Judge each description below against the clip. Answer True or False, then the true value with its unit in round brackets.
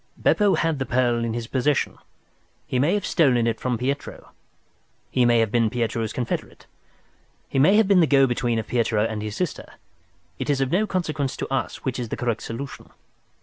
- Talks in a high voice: False (125 Hz)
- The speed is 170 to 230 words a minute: True (195 wpm)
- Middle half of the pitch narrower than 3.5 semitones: False (3.8 semitones)